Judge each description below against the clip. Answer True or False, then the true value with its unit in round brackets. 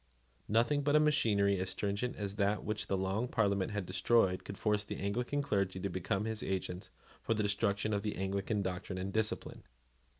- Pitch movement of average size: False (2.3 semitones)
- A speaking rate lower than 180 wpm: False (190 wpm)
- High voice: False (100 Hz)